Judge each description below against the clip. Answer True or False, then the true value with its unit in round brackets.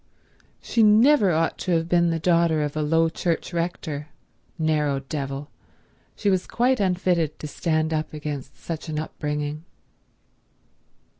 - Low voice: False (160 Hz)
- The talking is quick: False (135 wpm)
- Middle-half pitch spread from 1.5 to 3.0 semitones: True (2.7 semitones)